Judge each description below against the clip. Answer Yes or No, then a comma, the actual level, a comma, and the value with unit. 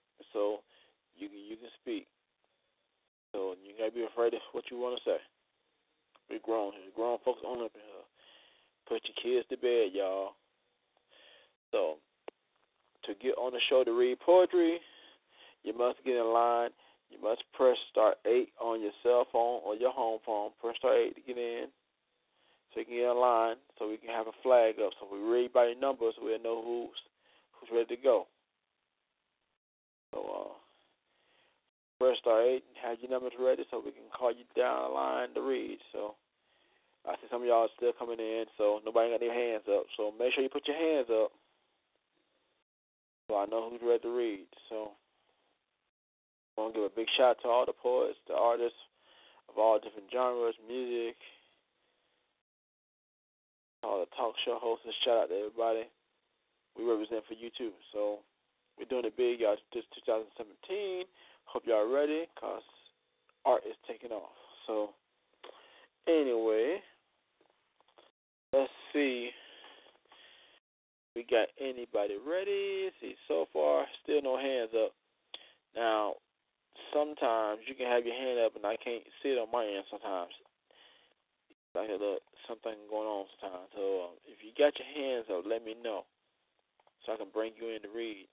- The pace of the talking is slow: No, average, 170 wpm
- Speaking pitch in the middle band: No, low, 120 Hz